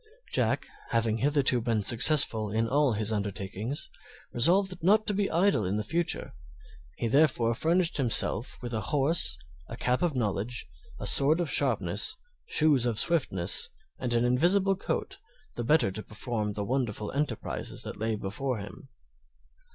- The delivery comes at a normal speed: Yes, average, 150 wpm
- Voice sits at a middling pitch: No, low, 120 Hz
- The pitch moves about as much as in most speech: No, wide, 6.2 semitones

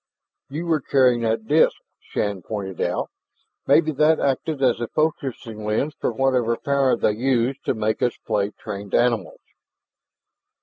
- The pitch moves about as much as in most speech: Yes, average, 4.2 semitones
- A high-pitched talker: No, low, 120 Hz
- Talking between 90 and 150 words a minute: Yes, average, 145 wpm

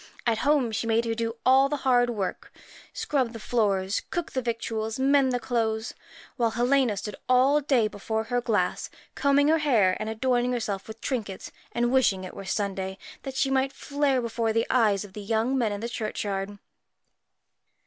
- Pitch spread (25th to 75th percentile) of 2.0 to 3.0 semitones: No, average, 3.5 semitones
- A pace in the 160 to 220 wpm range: Yes, average, 180 wpm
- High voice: Yes, high, 230 Hz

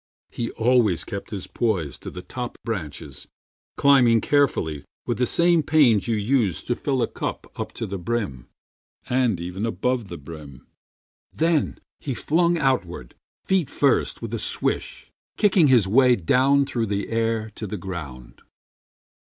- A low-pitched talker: Yes, low, 115 Hz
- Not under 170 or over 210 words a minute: No, average, 150 wpm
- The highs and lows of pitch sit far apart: Yes, wide, 6.4 semitones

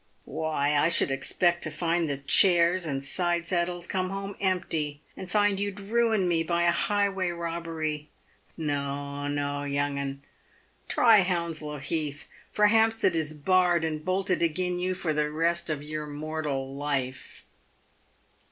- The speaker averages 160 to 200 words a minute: No, average, 145 wpm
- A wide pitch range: No, average, 4.0 semitones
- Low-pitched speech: No, medium, 165 Hz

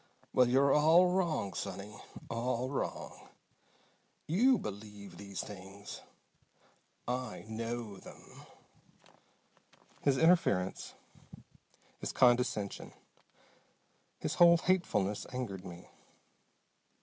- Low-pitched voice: Yes, low, 120 Hz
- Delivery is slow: Yes, slow, 80 wpm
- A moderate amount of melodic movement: No, wide, 6.7 semitones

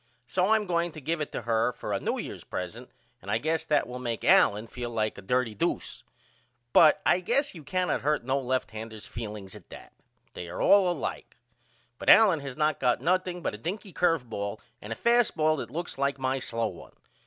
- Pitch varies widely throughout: Yes, wide, 7.2 semitones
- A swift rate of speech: Yes, fast, 215 wpm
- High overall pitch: No, low, 135 Hz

